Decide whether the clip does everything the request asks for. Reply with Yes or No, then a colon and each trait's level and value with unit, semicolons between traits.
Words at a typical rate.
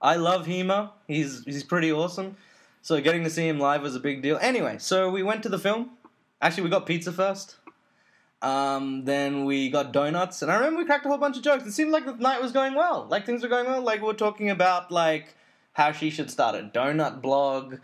No: fast, 235 wpm